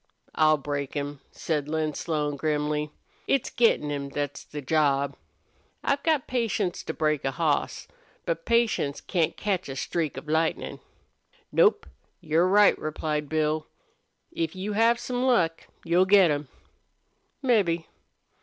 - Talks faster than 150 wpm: No, slow, 135 wpm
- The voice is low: No, medium, 155 Hz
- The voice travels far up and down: No, average, 4.5 semitones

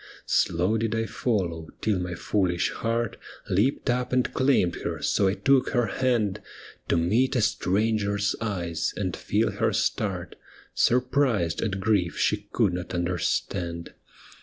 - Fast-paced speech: No, average, 140 wpm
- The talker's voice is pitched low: Yes, low, 105 Hz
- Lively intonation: No, average, 4.9 semitones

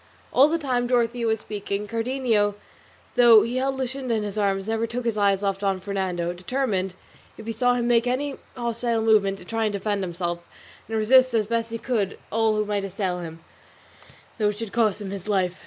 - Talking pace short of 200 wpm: No, fast, 205 wpm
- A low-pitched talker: No, high, 220 Hz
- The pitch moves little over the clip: No, average, 3.3 semitones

